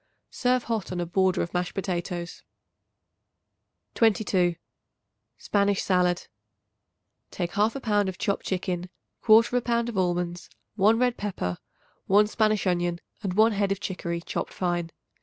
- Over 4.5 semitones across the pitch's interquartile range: No, average, 3.4 semitones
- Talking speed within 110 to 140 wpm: Yes, slow, 135 wpm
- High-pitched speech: Yes, high, 195 Hz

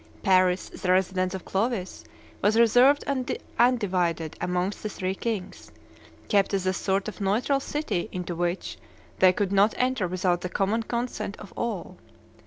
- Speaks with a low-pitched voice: No, high, 195 Hz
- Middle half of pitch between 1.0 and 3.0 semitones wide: No, average, 3.8 semitones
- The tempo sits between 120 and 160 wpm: Yes, average, 155 wpm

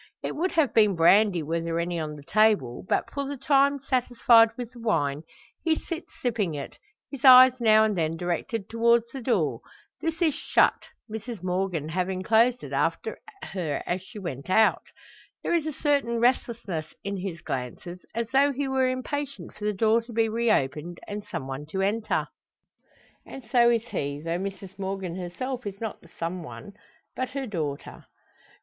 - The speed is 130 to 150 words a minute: No, average, 180 wpm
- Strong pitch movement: Yes, wide, 6.2 semitones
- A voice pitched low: No, high, 215 Hz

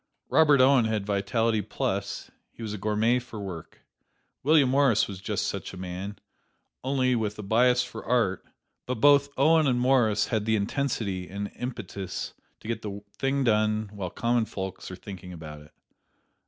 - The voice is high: No, low, 110 Hz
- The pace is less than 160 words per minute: No, average, 170 wpm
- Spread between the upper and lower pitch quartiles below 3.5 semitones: No, average, 4.1 semitones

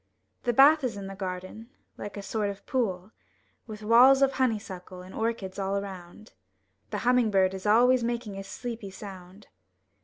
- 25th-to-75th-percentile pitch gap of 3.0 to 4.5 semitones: Yes, average, 3.7 semitones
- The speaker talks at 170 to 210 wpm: Yes, average, 175 wpm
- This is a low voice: No, high, 210 Hz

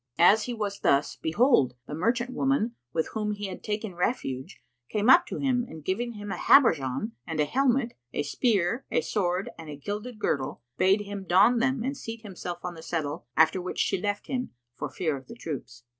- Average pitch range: No, wide, 6.6 semitones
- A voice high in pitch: Yes, high, 205 Hz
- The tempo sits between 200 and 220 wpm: Yes, fast, 205 wpm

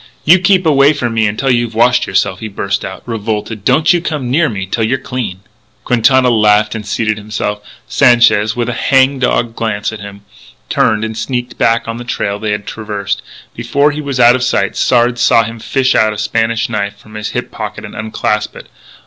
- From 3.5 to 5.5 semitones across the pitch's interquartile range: No, average, 2.9 semitones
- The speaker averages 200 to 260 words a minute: Yes, fast, 205 wpm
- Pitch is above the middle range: No, low, 115 Hz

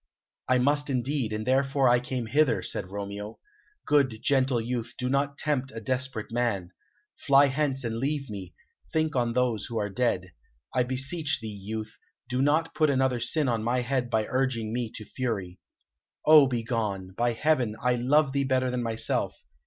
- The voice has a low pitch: Yes, low, 125 Hz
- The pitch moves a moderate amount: Yes, average, 3.4 semitones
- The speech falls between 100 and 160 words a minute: No, average, 175 wpm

